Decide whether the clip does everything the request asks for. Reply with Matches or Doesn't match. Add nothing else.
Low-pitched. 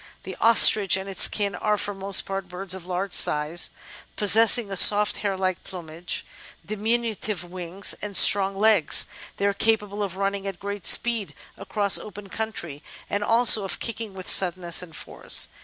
Doesn't match